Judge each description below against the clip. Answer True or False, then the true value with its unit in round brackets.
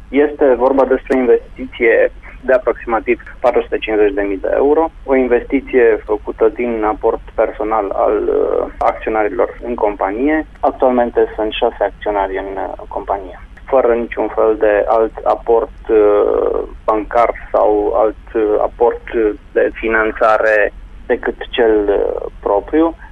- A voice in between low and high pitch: True (150 Hz)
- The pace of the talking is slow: True (105 wpm)